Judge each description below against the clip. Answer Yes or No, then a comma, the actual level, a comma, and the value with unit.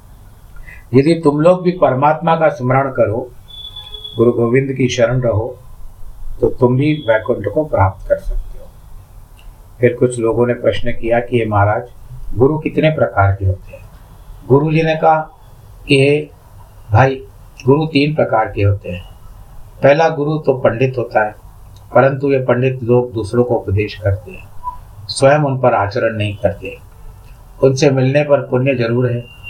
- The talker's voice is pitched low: Yes, low, 120 Hz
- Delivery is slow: No, average, 155 wpm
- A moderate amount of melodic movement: Yes, average, 4.8 semitones